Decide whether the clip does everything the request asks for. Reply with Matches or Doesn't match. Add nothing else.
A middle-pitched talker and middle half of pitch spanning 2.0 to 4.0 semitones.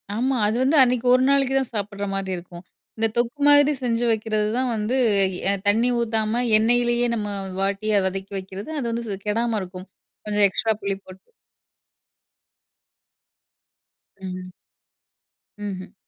Doesn't match